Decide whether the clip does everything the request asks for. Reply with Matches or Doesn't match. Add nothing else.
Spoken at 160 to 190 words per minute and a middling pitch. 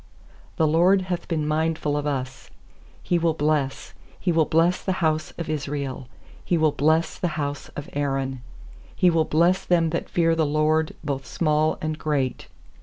Matches